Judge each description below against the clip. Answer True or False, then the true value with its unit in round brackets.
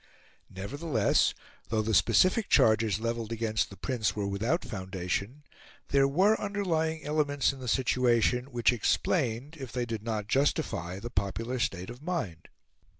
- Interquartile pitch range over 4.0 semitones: True (5.0 semitones)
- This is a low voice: True (120 Hz)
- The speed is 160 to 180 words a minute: False (145 wpm)